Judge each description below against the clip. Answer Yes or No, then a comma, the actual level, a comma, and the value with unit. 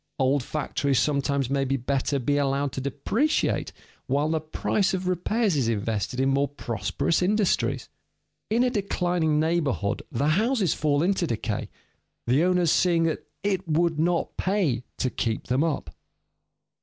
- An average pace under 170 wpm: Yes, average, 145 wpm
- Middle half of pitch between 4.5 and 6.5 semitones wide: Yes, average, 4.9 semitones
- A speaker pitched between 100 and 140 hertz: No, medium, 150 Hz